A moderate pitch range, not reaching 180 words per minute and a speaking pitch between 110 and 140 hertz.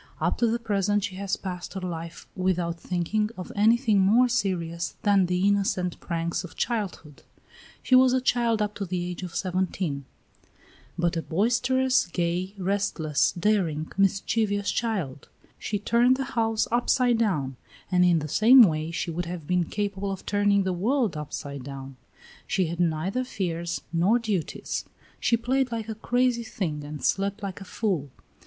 No: average, 4.6 semitones; average, 165 wpm; high, 195 Hz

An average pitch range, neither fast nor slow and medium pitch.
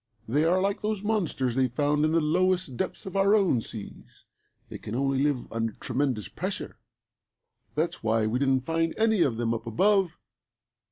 No: wide, 7.5 semitones; average, 175 wpm; medium, 145 Hz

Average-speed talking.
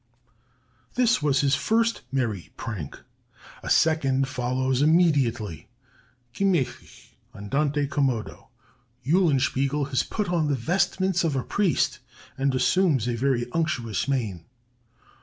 No: slow, 110 wpm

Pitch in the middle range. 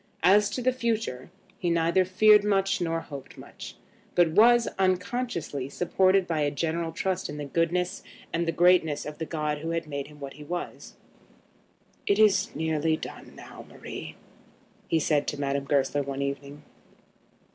Yes: medium, 165 Hz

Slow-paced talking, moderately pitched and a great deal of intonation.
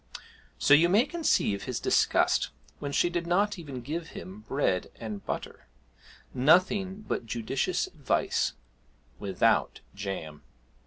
Yes: slow, 120 wpm; medium, 155 Hz; wide, 8.3 semitones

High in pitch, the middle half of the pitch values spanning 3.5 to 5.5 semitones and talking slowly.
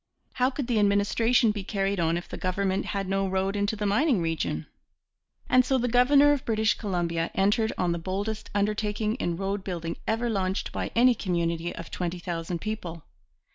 No: high, 200 Hz; average, 4.0 semitones; average, 175 wpm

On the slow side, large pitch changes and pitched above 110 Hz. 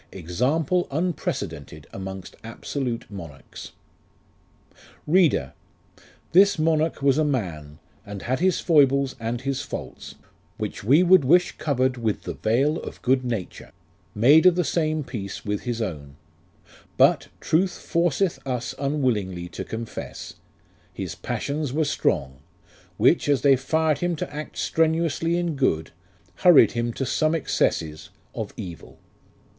Yes: slow, 130 wpm; wide, 7.3 semitones; low, 135 Hz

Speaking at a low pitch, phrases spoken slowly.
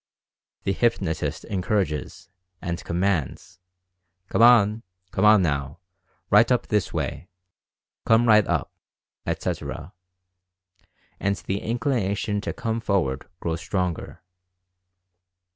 Yes: low, 100 Hz; slow, 110 wpm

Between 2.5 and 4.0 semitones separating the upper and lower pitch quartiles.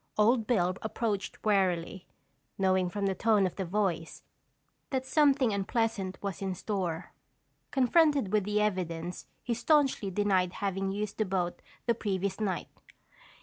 Yes: average, 3.0 semitones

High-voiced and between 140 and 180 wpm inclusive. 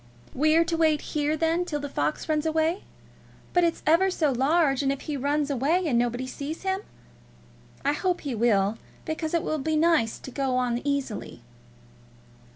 Yes: very high, 295 Hz; average, 175 wpm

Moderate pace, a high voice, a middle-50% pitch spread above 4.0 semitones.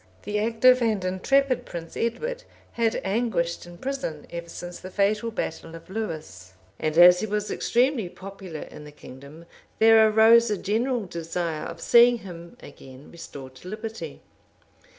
Yes: average, 150 wpm; high, 195 Hz; average, 5.3 semitones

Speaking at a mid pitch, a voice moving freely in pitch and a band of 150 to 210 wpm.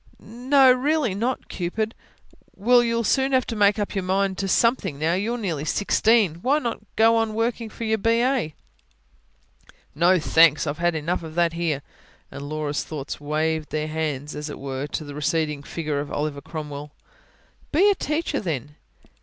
Yes: medium, 175 Hz; wide, 7.1 semitones; average, 170 wpm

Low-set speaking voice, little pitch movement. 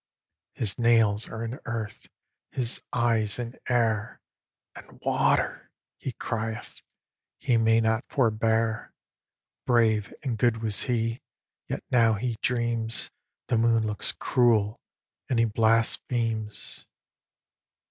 Yes: low, 115 Hz; narrow, 1.2 semitones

